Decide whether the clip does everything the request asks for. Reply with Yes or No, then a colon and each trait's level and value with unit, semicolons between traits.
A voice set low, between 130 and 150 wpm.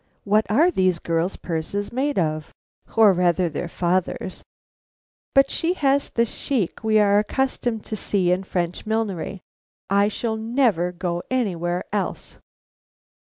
No: high, 200 Hz; slow, 135 wpm